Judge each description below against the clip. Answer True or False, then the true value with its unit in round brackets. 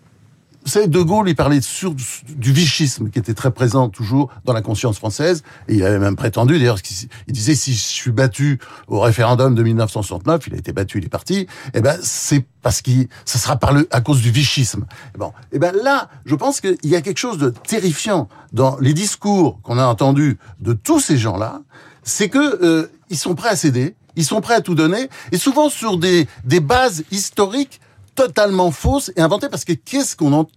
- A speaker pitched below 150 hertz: True (140 Hz)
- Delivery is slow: False (205 wpm)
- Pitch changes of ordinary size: False (6.6 semitones)